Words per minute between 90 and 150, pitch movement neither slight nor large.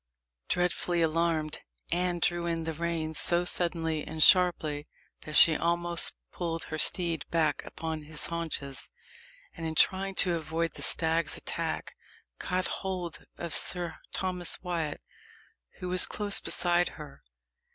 No: slow, 135 wpm; narrow, 1.8 semitones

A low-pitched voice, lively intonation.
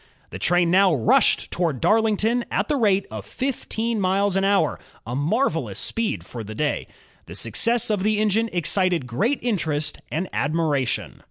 No: medium, 185 Hz; wide, 6.6 semitones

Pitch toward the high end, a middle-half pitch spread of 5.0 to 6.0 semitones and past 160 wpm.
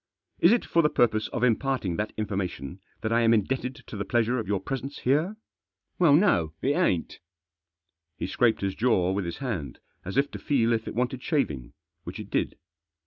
No: low, 115 Hz; wide, 5.5 semitones; average, 200 wpm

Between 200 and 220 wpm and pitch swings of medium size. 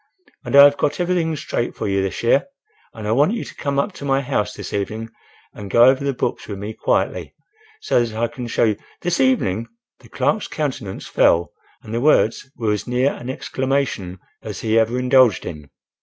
Yes: fast, 205 wpm; average, 4.5 semitones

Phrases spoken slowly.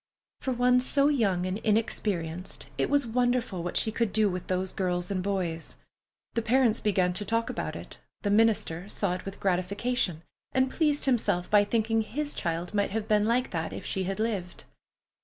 No: average, 185 wpm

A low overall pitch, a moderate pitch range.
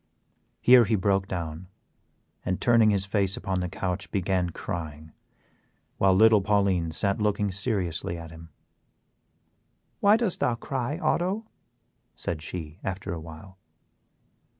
Yes: very low, 95 Hz; average, 3.7 semitones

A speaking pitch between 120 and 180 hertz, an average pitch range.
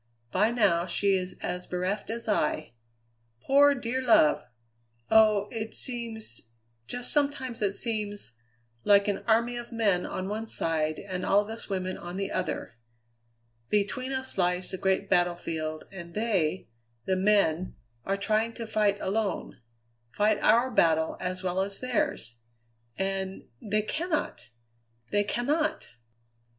No: high, 205 Hz; average, 3.8 semitones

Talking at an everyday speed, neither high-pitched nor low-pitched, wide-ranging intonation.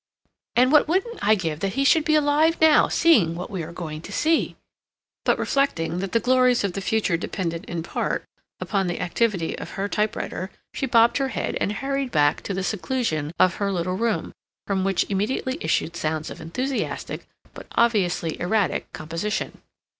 No: average, 175 wpm; high, 200 Hz; wide, 7.0 semitones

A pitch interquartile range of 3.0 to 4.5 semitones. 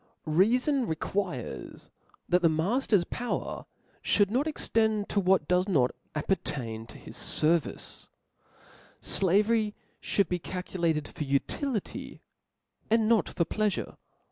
No: average, 5.3 semitones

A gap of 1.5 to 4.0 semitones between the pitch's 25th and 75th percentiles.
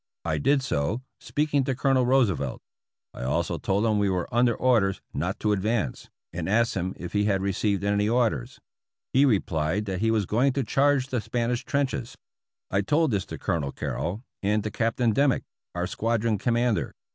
No: average, 4.4 semitones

